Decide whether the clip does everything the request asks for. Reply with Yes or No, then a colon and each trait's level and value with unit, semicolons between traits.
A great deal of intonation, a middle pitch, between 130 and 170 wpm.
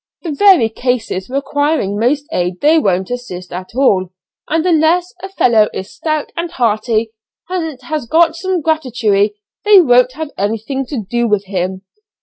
No: wide, 7.2 semitones; very high, 250 Hz; average, 155 wpm